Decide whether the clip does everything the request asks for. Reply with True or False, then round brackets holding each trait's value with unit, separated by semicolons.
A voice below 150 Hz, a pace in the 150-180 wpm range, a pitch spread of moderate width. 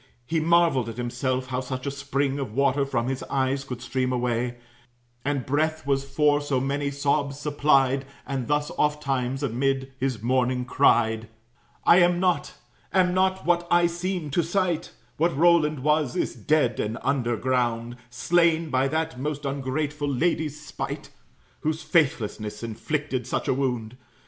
True (140 Hz; 155 wpm; 3.3 semitones)